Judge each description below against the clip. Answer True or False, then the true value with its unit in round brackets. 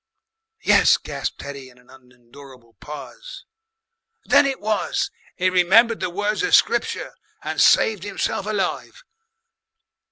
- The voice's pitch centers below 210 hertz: True (185 Hz)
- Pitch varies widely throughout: True (8.4 semitones)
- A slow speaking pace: True (120 wpm)